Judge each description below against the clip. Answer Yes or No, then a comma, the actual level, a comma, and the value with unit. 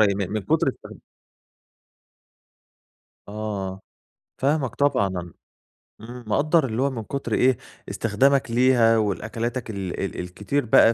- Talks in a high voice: No, low, 115 Hz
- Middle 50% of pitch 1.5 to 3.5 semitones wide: No, average, 4.3 semitones